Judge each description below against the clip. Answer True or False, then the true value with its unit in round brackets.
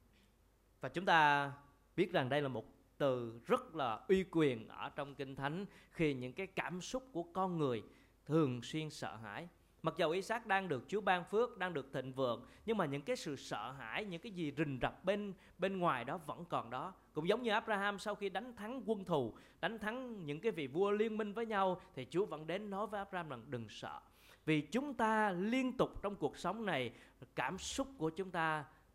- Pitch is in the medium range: True (180 Hz)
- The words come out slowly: False (220 wpm)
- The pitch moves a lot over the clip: True (6.0 semitones)